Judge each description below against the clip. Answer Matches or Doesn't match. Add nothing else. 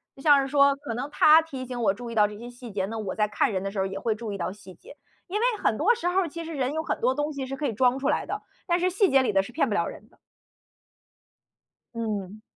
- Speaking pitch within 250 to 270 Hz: Matches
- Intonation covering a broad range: Matches